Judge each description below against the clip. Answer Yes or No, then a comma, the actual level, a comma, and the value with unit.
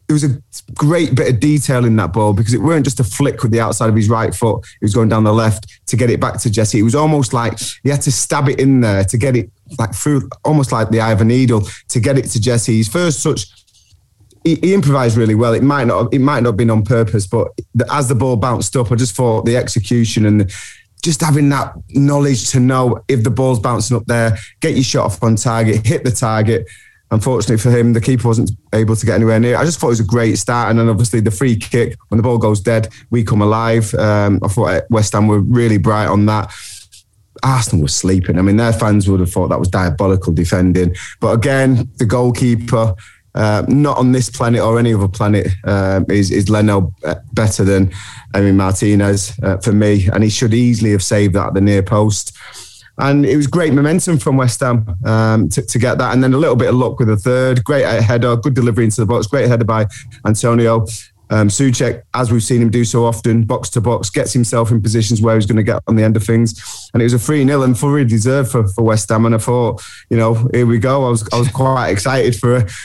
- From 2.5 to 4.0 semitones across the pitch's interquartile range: Yes, average, 2.8 semitones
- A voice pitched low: Yes, low, 115 Hz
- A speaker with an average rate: No, fast, 245 wpm